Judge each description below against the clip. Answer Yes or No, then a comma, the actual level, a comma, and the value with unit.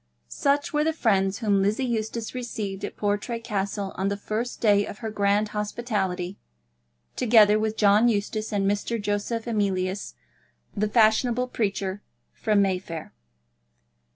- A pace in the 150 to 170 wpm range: No, slow, 135 wpm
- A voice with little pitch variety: Yes, narrow, 2.3 semitones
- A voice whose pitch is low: No, high, 210 Hz